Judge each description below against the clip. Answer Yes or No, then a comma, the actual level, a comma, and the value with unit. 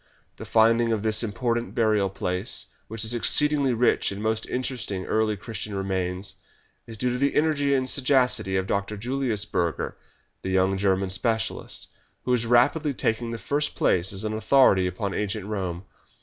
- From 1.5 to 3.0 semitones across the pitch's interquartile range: No, average, 4.0 semitones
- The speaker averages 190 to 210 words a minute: No, average, 165 wpm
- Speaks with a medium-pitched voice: No, low, 110 Hz